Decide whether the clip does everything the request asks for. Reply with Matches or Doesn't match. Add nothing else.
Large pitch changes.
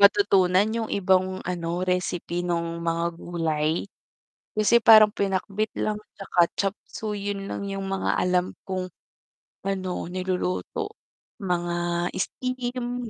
Doesn't match